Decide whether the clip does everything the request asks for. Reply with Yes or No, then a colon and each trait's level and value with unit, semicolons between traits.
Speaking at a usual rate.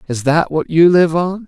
No: fast, 245 wpm